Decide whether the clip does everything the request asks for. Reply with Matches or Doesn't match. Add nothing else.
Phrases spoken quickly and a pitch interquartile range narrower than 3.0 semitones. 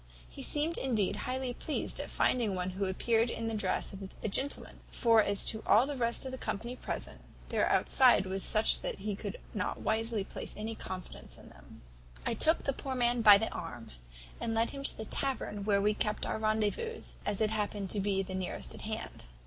Doesn't match